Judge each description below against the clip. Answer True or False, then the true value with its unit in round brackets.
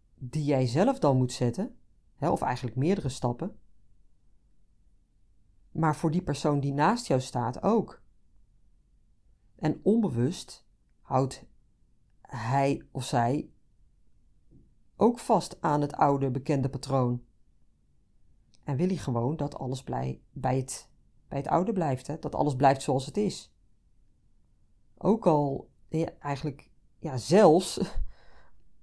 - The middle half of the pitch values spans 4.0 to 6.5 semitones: True (5.1 semitones)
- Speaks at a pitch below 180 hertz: True (135 Hz)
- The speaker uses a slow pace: True (125 wpm)